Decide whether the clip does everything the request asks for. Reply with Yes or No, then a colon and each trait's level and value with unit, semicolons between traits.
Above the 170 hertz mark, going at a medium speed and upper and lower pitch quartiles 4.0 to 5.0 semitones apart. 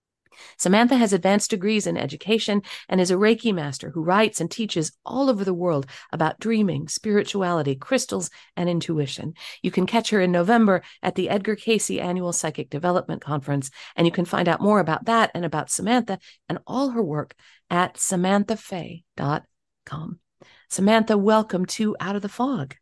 Yes: medium, 185 Hz; average, 165 wpm; average, 4.3 semitones